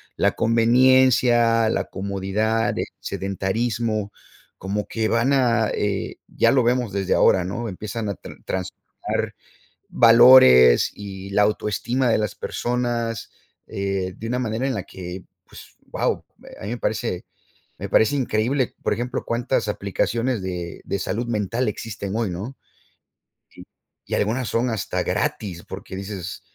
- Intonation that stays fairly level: No, average, 3.4 semitones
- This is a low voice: Yes, low, 110 Hz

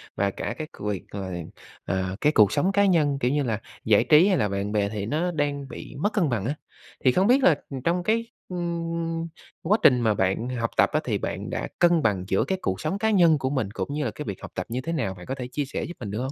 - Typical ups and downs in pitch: No, wide, 8.1 semitones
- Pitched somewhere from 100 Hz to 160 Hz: Yes, medium, 140 Hz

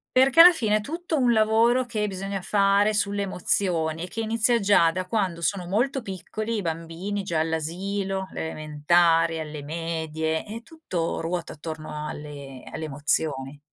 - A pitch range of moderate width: Yes, average, 5.0 semitones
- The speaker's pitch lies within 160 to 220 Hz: Yes, medium, 185 Hz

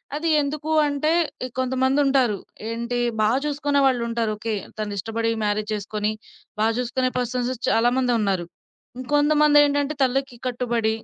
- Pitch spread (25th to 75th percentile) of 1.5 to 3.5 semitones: No, average, 3.9 semitones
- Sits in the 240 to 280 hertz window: Yes, very high, 250 Hz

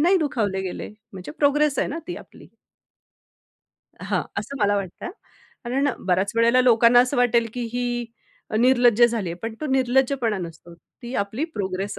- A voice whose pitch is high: Yes, high, 240 Hz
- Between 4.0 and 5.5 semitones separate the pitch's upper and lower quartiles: Yes, average, 4.4 semitones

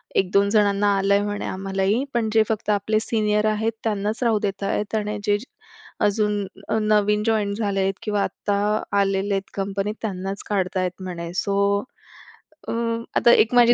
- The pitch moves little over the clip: Yes, narrow, 1.5 semitones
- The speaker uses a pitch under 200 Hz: No, high, 205 Hz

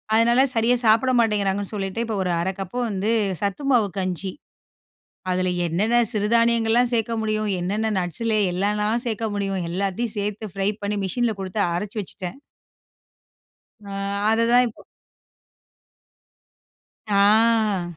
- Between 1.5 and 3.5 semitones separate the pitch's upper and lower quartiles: Yes, average, 2.8 semitones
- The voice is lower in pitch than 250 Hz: Yes, high, 210 Hz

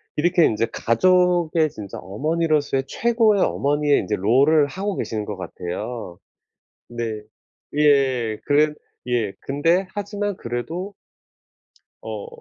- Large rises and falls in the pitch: Yes, wide, 7.2 semitones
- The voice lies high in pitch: No, medium, 145 Hz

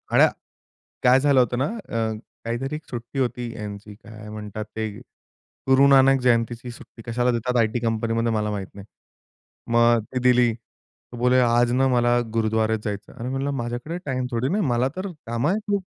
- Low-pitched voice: Yes, low, 120 Hz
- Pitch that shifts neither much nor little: No, narrow, 2.2 semitones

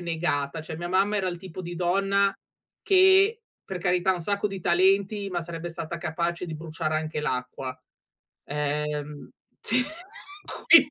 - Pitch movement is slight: No, average, 3.7 semitones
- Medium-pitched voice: Yes, medium, 175 Hz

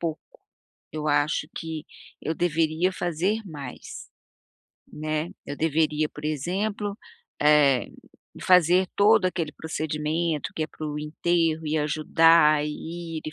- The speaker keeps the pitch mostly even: Yes, narrow, 2.2 semitones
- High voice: No, medium, 155 Hz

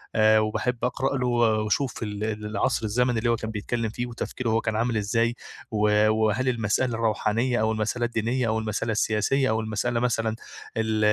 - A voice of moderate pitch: No, low, 110 Hz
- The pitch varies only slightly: Yes, narrow, 1.9 semitones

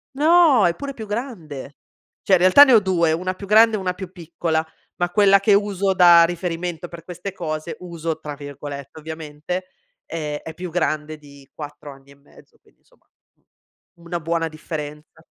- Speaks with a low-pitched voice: No, medium, 170 Hz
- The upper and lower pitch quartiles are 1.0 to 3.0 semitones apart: No, average, 3.7 semitones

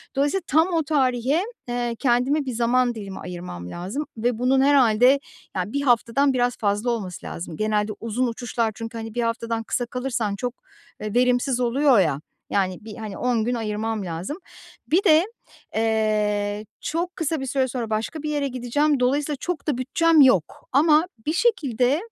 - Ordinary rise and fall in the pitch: Yes, average, 4.4 semitones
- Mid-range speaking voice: No, high, 245 Hz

